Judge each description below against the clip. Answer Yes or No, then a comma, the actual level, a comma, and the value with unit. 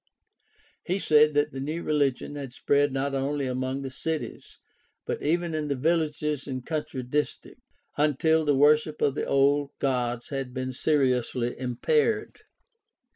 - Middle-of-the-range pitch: Yes, medium, 145 Hz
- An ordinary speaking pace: Yes, average, 145 wpm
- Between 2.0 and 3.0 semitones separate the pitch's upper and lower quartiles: Yes, narrow, 2.6 semitones